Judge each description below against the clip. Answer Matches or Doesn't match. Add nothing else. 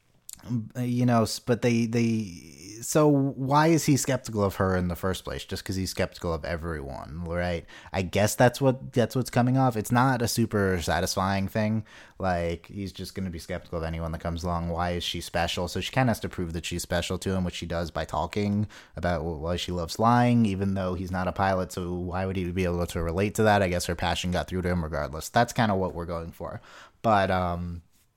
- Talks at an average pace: Doesn't match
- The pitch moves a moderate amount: Matches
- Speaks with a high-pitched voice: Doesn't match